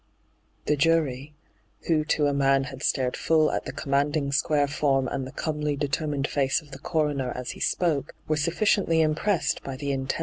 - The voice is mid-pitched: Yes, medium, 145 Hz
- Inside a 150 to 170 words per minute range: No, average, 180 wpm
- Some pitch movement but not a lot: No, narrow, 2.1 semitones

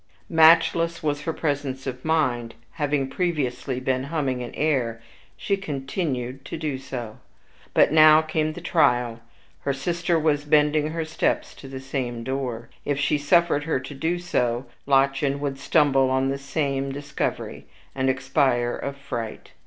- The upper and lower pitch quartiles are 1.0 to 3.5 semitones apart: Yes, average, 2.9 semitones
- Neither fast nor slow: Yes, average, 155 wpm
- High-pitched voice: No, medium, 140 Hz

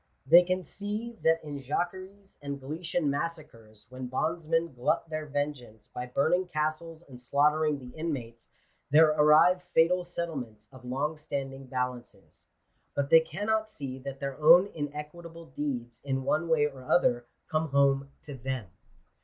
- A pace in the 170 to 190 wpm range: No, average, 150 wpm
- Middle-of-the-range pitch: Yes, medium, 150 Hz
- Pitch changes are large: No, average, 3.9 semitones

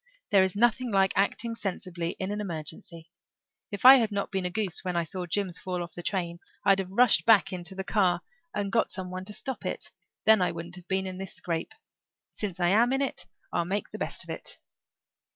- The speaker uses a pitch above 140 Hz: Yes, high, 190 Hz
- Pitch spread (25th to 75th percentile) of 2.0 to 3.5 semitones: Yes, average, 2.8 semitones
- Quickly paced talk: Yes, fast, 225 wpm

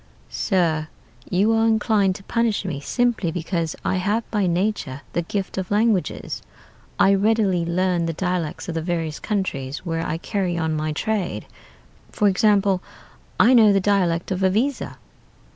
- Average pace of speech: Yes, average, 155 wpm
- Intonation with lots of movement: No, average, 3.8 semitones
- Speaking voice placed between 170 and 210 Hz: Yes, high, 190 Hz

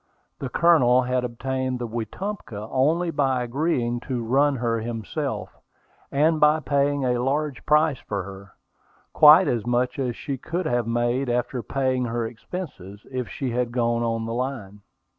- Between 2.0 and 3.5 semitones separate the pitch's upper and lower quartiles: Yes, average, 3.0 semitones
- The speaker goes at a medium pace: Yes, average, 160 wpm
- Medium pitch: No, low, 125 Hz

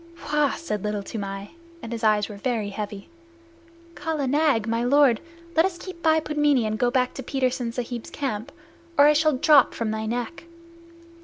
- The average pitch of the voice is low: No, high, 245 Hz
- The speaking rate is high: No, average, 170 wpm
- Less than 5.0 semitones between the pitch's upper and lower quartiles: No, average, 5.3 semitones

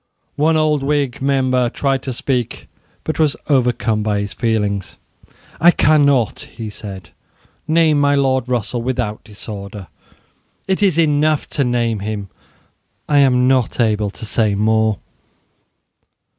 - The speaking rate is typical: No, slow, 130 wpm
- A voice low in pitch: Yes, low, 125 Hz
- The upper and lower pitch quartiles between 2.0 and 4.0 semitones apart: No, average, 4.8 semitones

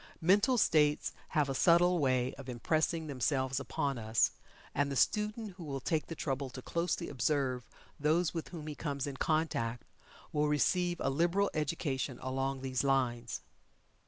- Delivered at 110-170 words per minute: Yes, average, 160 wpm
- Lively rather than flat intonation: No, average, 4.0 semitones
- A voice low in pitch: No, medium, 145 Hz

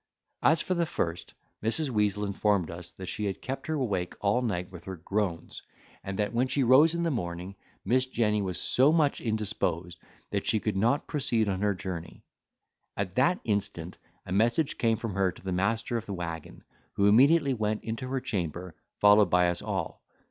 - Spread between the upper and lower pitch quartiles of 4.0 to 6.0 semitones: Yes, average, 5.2 semitones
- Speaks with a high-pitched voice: No, low, 105 Hz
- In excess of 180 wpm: Yes, average, 190 wpm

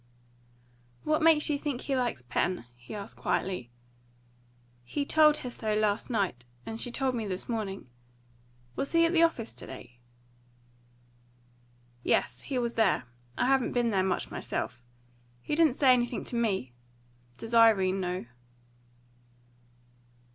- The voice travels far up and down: Yes, wide, 6.0 semitones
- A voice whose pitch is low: No, high, 230 Hz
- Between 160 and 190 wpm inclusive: No, average, 140 wpm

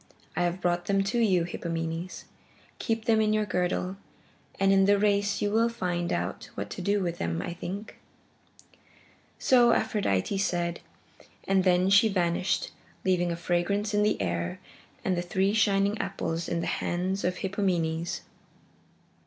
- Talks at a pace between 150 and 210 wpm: Yes, average, 155 wpm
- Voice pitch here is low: No, medium, 185 Hz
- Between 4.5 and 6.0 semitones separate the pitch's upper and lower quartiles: No, average, 2.8 semitones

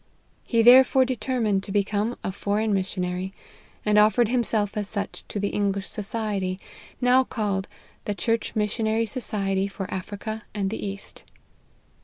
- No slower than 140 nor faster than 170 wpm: Yes, average, 150 wpm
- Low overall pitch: No, high, 210 Hz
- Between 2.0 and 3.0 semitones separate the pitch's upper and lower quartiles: Yes, narrow, 2.5 semitones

